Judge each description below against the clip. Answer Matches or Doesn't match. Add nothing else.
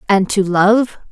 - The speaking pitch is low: Doesn't match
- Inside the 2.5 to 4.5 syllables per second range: Matches